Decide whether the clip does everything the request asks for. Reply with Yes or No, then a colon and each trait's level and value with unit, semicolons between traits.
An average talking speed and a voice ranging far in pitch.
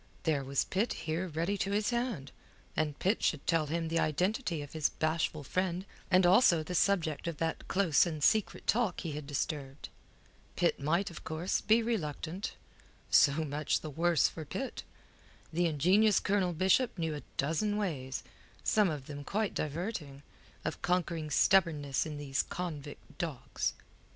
No: average, 160 wpm; average, 4.1 semitones